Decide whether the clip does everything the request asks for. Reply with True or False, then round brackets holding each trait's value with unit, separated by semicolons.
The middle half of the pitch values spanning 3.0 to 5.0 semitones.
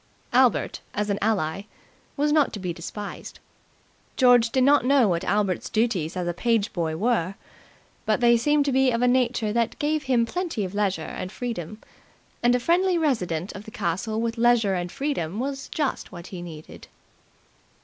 False (5.4 semitones)